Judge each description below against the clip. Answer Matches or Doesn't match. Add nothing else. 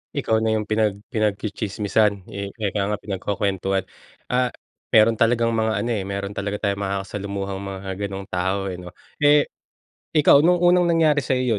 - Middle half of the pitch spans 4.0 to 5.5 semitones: Doesn't match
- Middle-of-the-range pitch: Doesn't match